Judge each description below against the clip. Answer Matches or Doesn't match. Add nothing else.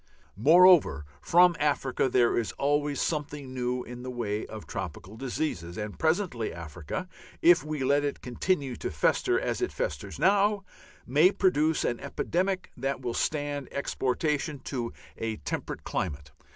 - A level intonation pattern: Doesn't match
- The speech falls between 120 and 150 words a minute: Matches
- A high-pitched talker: Doesn't match